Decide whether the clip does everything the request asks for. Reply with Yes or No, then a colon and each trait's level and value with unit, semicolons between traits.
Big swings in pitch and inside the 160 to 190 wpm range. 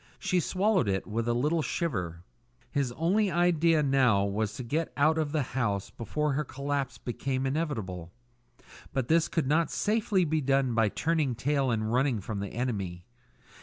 Yes: wide, 5.8 semitones; average, 165 wpm